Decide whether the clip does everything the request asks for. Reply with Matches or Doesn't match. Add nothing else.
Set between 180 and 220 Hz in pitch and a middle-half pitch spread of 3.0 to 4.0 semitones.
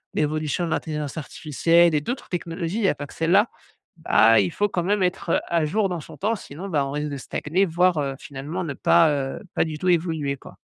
Doesn't match